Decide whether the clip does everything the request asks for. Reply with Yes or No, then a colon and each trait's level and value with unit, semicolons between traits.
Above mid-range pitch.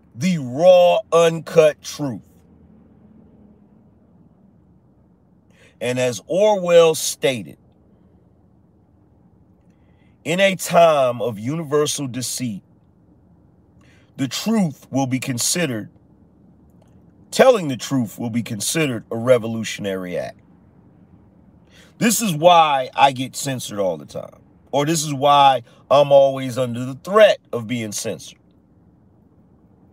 No: medium, 140 Hz